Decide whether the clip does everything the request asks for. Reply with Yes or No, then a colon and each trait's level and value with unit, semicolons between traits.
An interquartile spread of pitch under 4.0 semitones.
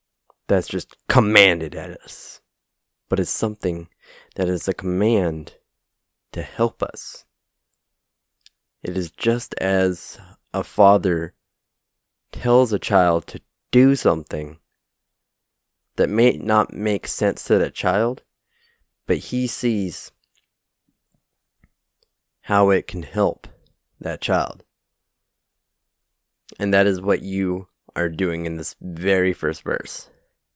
Yes: average, 3.4 semitones